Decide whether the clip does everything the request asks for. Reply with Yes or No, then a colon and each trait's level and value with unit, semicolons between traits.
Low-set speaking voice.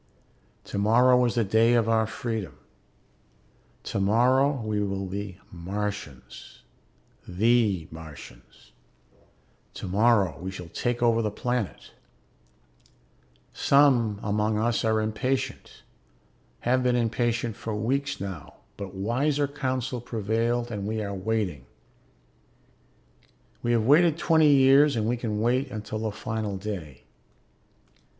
Yes: low, 110 Hz